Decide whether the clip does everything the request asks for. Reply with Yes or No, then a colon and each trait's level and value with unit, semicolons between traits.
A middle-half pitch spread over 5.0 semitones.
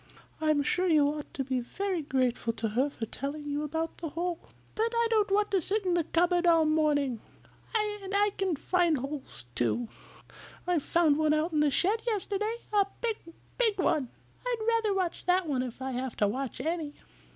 Yes: wide, 5.6 semitones